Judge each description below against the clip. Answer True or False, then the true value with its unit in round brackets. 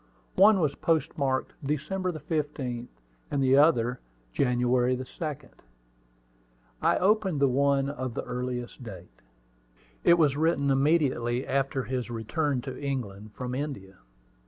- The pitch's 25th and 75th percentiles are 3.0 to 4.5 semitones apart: True (3.4 semitones)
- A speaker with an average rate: False (120 wpm)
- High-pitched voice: False (135 Hz)